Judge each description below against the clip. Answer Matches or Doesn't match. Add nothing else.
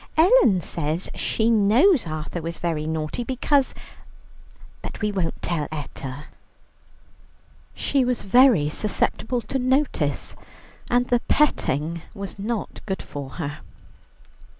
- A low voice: Doesn't match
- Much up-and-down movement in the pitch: Matches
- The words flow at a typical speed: Doesn't match